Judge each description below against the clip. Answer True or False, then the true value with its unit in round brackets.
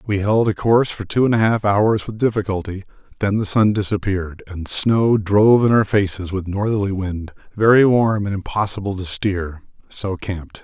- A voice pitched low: True (100 Hz)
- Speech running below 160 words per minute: False (180 wpm)